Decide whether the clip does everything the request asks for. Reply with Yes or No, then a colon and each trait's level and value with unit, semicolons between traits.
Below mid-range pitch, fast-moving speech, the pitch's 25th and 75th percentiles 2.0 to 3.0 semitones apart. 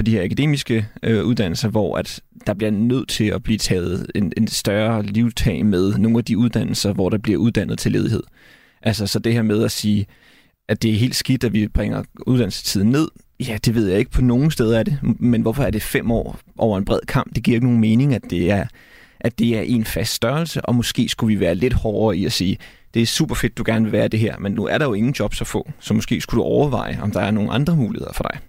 Yes: low, 115 Hz; fast, 255 wpm; narrow, 2.4 semitones